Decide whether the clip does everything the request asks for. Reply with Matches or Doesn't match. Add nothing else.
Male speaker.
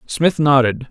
Matches